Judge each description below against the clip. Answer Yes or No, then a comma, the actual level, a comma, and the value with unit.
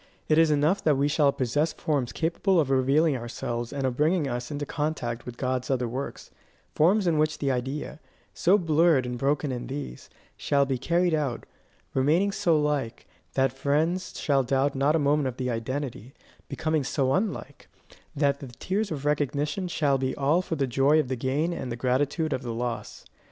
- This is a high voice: No, medium, 140 Hz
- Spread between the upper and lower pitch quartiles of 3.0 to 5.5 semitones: Yes, average, 3.3 semitones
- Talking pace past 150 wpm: Yes, average, 190 wpm